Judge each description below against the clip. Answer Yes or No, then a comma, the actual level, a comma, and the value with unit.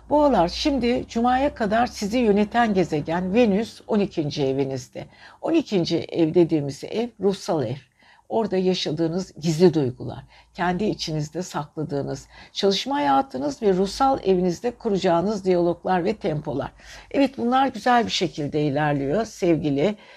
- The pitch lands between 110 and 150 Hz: No, medium, 185 Hz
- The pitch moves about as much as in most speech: No, wide, 6.8 semitones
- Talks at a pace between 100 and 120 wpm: Yes, average, 115 wpm